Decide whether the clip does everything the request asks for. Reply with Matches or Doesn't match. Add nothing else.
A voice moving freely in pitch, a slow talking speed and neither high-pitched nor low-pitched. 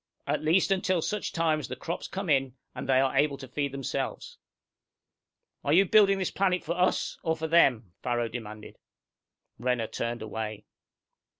Doesn't match